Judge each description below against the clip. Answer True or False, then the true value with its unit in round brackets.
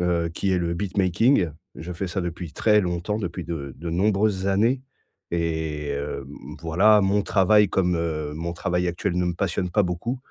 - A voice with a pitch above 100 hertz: False (90 Hz)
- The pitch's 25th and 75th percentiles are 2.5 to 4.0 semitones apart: True (2.9 semitones)